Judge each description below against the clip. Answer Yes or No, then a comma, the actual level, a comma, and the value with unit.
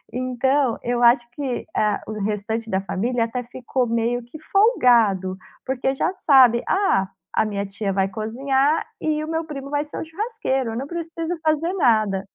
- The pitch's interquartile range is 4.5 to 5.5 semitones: Yes, average, 5.1 semitones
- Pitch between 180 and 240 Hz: No, very high, 250 Hz